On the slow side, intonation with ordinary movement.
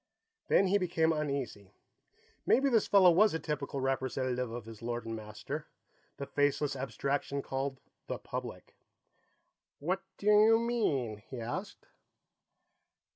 No: slow, 130 wpm; wide, 7.0 semitones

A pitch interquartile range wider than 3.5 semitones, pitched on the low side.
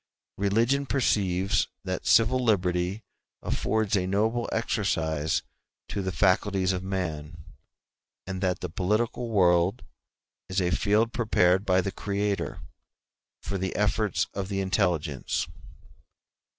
No: average, 2.9 semitones; very low, 95 Hz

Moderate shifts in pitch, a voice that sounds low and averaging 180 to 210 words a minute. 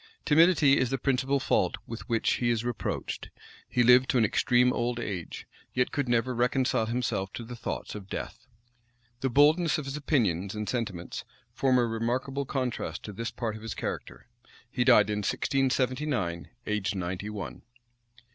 No: average, 3.8 semitones; low, 120 Hz; average, 165 wpm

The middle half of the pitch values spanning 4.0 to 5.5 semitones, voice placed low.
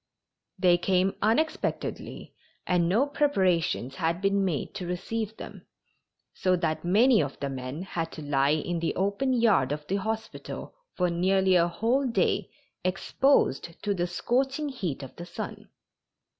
No: average, 4.7 semitones; medium, 185 Hz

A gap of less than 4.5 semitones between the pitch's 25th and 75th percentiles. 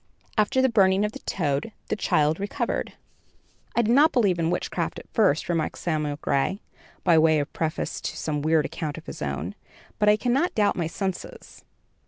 No: average, 5.2 semitones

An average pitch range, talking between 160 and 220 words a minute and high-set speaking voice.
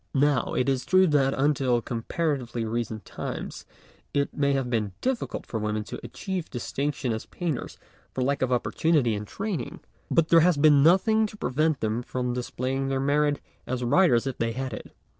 No: average, 4.1 semitones; average, 185 wpm; low, 135 Hz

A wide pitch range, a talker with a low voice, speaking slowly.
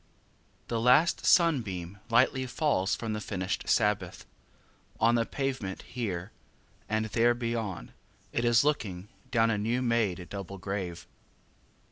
No: average, 3.7 semitones; low, 115 Hz; slow, 125 wpm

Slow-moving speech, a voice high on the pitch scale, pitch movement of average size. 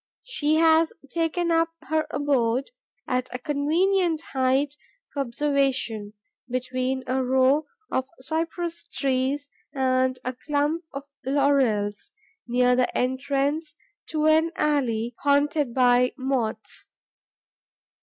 Yes: slow, 105 wpm; very high, 275 Hz; average, 3.2 semitones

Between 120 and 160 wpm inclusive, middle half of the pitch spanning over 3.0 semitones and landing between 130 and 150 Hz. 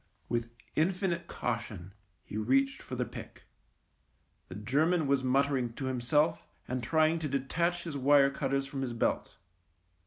Yes: average, 150 wpm; average, 4.1 semitones; low, 135 Hz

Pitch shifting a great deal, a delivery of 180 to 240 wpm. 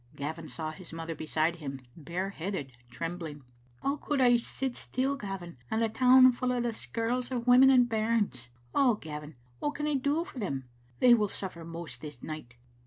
Yes: wide, 8.0 semitones; average, 190 wpm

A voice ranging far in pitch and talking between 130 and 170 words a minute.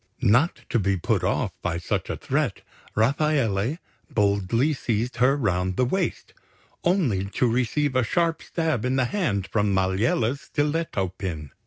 Yes: wide, 6.8 semitones; average, 150 wpm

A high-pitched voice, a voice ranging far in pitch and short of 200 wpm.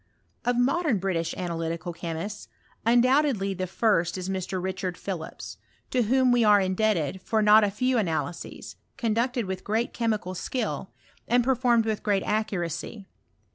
No: high, 210 Hz; average, 4.4 semitones; average, 150 wpm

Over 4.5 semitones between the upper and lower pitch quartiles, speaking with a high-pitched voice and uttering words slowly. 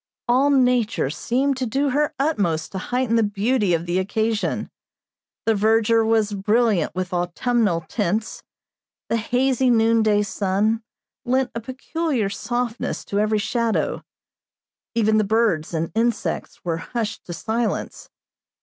No: average, 3.4 semitones; high, 225 Hz; slow, 130 wpm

